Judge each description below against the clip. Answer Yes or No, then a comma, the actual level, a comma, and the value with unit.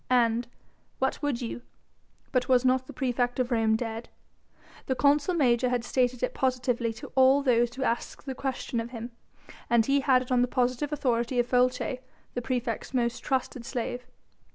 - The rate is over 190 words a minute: No, average, 175 wpm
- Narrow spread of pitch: Yes, narrow, 1.5 semitones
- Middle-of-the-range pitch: No, very high, 250 Hz